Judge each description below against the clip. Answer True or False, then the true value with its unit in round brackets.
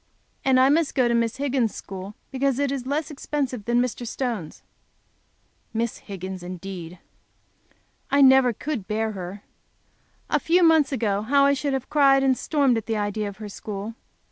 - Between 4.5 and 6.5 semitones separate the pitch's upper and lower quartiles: True (5.0 semitones)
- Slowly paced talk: False (170 wpm)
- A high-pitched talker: True (245 Hz)